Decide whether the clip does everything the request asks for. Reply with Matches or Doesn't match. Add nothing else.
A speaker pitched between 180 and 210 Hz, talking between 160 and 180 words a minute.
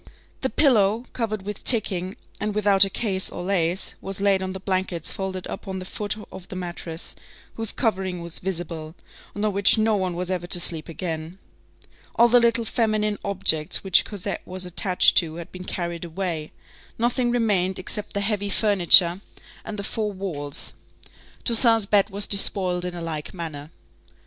Matches